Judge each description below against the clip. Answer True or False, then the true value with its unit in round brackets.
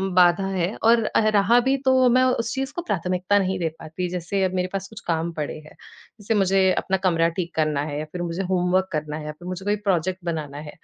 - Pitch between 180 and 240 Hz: True (185 Hz)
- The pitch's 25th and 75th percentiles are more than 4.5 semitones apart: False (3.4 semitones)